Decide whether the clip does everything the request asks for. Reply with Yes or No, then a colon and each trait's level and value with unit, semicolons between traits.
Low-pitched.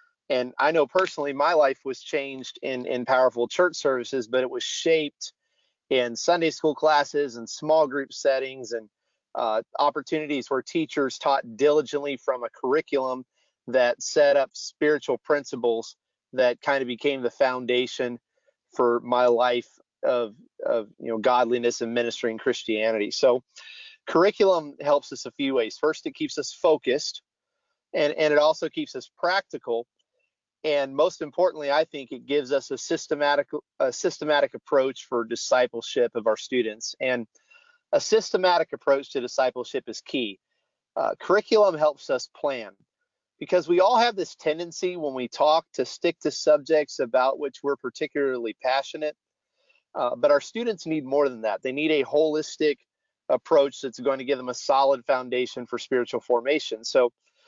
No: medium, 145 Hz